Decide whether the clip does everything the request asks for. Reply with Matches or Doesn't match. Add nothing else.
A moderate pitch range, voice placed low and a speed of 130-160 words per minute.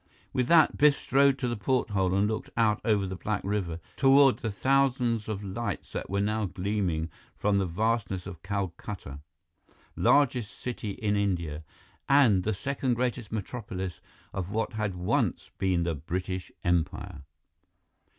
Matches